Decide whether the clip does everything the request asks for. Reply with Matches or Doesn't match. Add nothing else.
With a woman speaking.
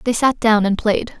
Matches